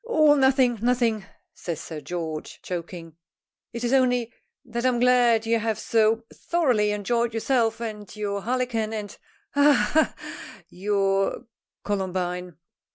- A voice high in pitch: Yes, high, 225 Hz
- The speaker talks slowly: Yes, slow, 130 wpm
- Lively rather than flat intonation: No, average, 4.0 semitones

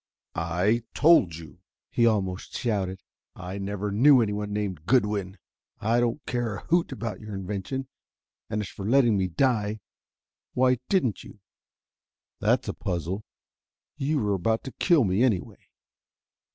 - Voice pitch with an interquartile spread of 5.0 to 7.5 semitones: No, average, 4.1 semitones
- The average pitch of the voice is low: Yes, low, 105 Hz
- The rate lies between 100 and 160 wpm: Yes, average, 140 wpm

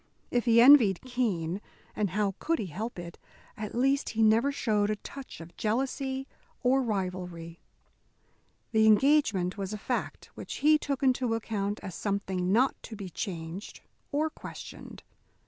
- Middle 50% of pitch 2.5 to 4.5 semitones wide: No, average, 5.1 semitones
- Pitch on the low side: No, high, 215 Hz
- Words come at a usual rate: Yes, average, 150 wpm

